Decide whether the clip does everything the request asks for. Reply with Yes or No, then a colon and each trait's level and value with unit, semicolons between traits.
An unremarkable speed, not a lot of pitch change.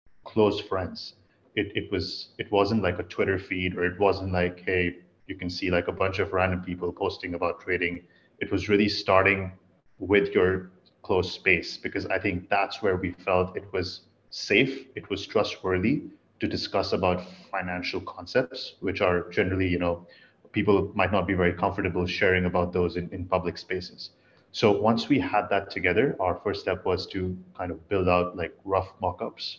Yes: average, 185 wpm; narrow, 1.5 semitones